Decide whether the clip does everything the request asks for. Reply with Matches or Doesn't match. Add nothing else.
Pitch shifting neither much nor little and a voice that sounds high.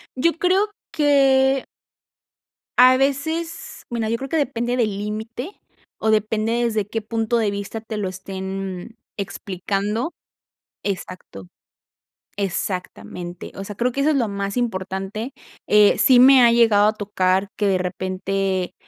Matches